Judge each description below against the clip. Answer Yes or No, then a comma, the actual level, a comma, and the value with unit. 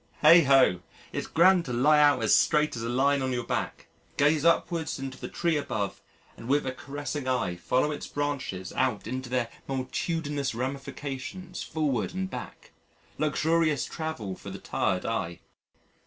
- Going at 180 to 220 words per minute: No, average, 160 wpm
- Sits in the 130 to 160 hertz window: Yes, medium, 140 Hz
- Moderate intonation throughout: Yes, average, 3.5 semitones